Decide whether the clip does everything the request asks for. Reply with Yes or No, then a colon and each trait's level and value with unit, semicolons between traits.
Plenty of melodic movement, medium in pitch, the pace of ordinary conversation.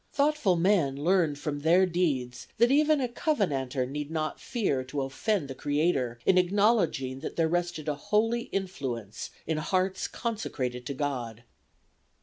Yes: wide, 6.6 semitones; medium, 160 Hz; average, 145 wpm